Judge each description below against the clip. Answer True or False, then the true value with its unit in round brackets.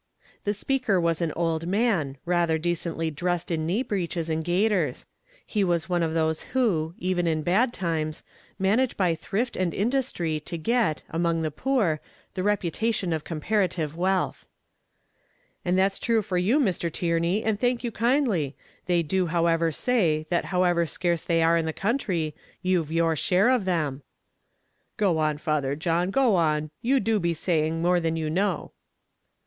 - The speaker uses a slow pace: False (165 wpm)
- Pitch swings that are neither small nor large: True (3.8 semitones)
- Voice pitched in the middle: True (175 Hz)